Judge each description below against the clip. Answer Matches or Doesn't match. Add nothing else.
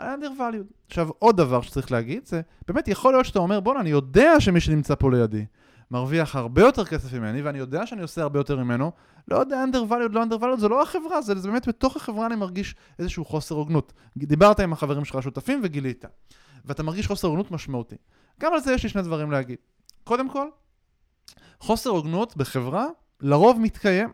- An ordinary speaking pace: Doesn't match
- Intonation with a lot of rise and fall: Matches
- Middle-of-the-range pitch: Matches